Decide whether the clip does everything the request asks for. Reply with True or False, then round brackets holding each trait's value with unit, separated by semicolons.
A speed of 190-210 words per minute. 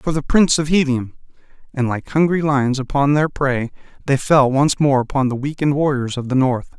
True (205 wpm)